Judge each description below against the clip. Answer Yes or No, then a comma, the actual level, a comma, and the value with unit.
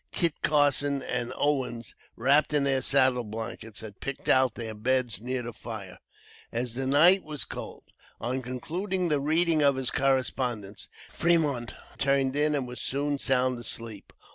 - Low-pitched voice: Yes, low, 130 Hz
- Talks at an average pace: Yes, average, 155 wpm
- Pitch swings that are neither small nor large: Yes, average, 3.3 semitones